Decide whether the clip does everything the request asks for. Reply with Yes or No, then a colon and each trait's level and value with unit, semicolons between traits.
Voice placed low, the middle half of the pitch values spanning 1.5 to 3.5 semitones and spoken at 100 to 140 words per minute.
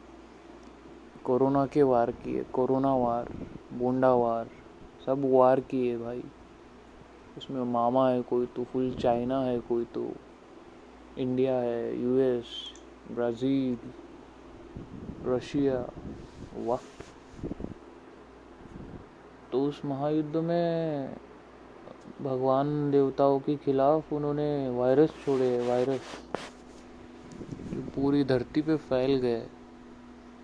No: low, 130 Hz; narrow, 2.4 semitones; average, 90 wpm